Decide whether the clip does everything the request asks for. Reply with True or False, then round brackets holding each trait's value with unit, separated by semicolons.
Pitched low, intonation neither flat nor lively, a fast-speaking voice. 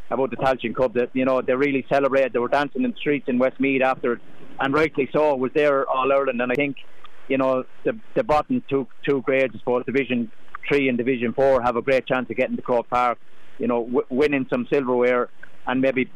False (130 Hz; 1.8 semitones; 230 wpm)